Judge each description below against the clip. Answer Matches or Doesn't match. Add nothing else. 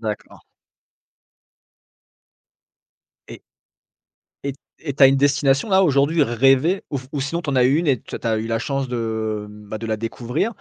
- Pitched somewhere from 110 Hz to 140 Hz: Matches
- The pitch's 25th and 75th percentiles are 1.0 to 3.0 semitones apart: Doesn't match